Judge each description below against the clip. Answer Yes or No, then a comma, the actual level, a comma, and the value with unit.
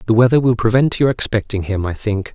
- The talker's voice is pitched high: No, low, 115 Hz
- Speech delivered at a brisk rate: Yes, fast, 230 wpm